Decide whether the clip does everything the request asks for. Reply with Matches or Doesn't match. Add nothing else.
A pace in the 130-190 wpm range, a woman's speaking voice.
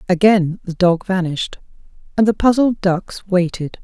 Matches